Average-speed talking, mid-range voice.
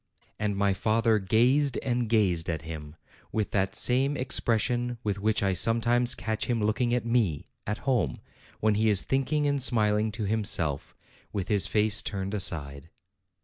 No: average, 160 wpm; low, 110 Hz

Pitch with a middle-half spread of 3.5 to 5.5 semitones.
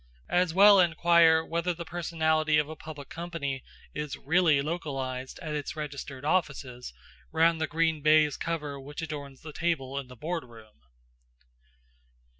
No: average, 3.0 semitones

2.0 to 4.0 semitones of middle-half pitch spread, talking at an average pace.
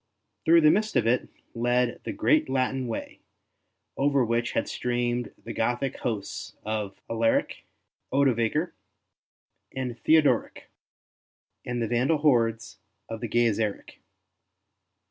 No: average, 3.2 semitones; slow, 110 wpm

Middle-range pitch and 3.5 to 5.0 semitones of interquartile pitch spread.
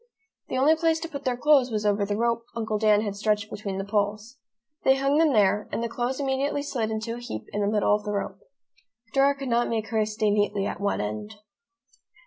No: high, 220 Hz; average, 4.2 semitones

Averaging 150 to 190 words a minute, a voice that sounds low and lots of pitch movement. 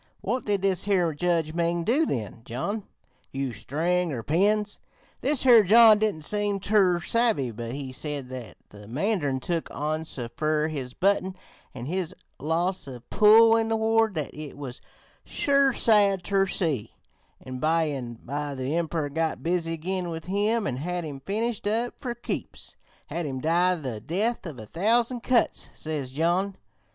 No: average, 170 wpm; medium, 170 Hz; wide, 6.4 semitones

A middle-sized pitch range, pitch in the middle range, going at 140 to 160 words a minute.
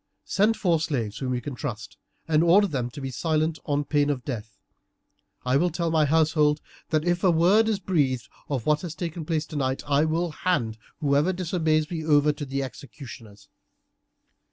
No: average, 3.8 semitones; medium, 150 Hz; average, 180 wpm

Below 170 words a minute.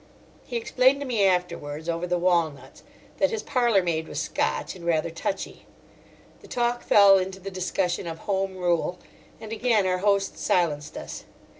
Yes: average, 160 wpm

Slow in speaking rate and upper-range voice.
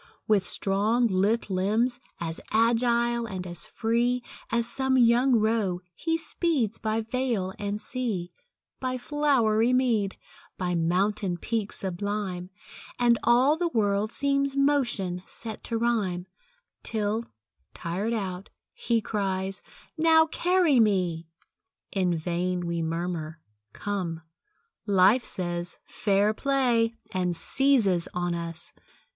Yes: slow, 115 wpm; high, 215 Hz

